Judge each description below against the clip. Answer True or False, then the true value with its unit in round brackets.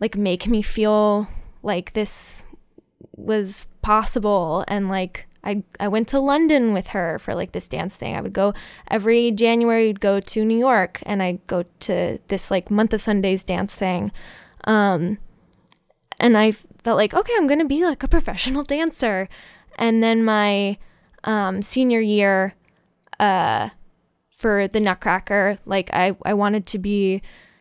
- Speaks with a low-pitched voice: False (210 Hz)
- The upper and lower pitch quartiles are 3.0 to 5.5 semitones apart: False (2.5 semitones)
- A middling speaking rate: True (155 wpm)